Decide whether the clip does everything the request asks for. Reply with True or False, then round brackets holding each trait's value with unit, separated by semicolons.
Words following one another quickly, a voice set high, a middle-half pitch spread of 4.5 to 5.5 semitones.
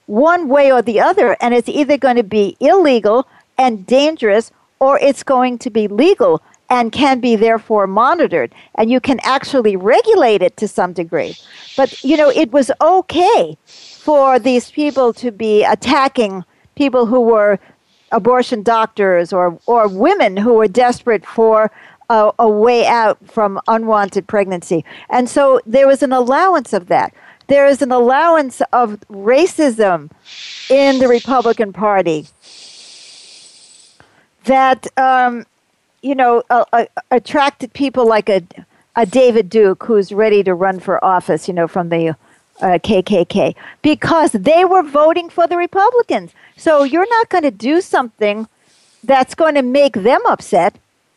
False (150 wpm; 245 Hz; 4.8 semitones)